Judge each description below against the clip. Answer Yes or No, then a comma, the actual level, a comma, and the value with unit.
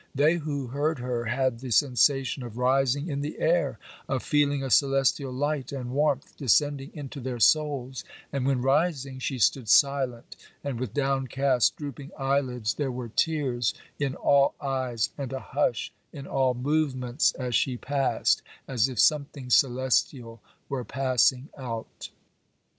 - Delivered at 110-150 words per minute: Yes, average, 145 wpm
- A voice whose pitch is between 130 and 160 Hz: Yes, low, 135 Hz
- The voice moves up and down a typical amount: No, narrow, 2.1 semitones